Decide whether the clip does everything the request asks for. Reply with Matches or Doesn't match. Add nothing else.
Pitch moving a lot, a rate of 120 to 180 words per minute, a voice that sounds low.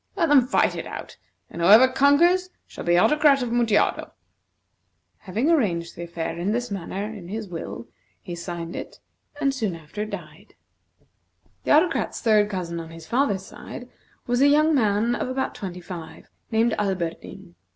Doesn't match